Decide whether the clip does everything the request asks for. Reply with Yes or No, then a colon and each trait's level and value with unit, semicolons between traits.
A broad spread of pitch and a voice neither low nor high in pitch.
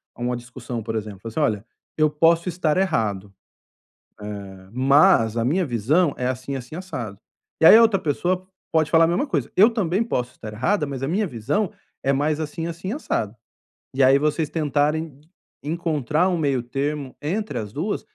Yes: wide, 5.8 semitones; medium, 150 Hz